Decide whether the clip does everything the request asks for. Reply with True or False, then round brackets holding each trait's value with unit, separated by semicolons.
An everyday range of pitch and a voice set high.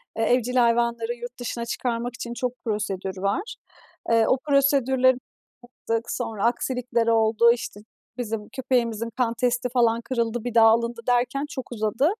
False (1.6 semitones; 235 Hz)